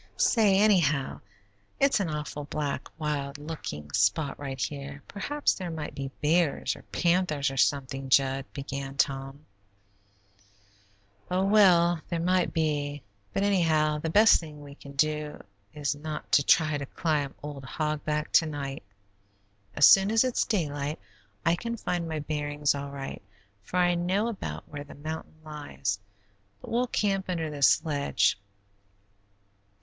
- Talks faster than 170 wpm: No, average, 145 wpm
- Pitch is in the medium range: Yes, medium, 150 Hz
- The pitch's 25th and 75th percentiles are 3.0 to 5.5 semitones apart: Yes, average, 3.7 semitones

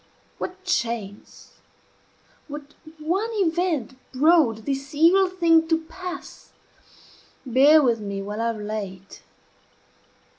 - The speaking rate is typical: No, slow, 100 wpm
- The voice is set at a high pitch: Yes, very high, 290 Hz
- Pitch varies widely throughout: Yes, wide, 6.9 semitones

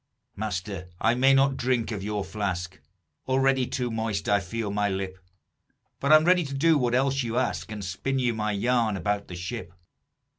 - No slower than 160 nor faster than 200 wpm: Yes, average, 185 wpm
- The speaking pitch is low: Yes, low, 110 Hz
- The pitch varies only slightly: No, average, 4.6 semitones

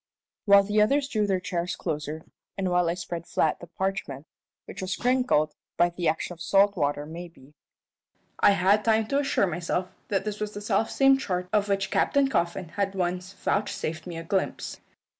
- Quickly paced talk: No, average, 180 wpm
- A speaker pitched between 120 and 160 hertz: No, medium, 185 Hz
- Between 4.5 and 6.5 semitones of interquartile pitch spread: No, average, 3.3 semitones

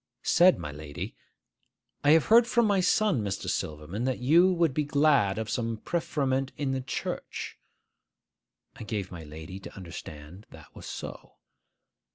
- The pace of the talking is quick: No, average, 155 wpm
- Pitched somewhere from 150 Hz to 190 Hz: No, low, 130 Hz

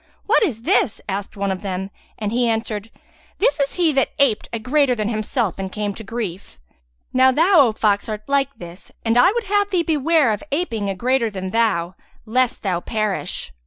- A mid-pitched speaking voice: No, high, 225 Hz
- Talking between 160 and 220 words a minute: Yes, average, 200 wpm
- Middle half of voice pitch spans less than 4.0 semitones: No, wide, 5.5 semitones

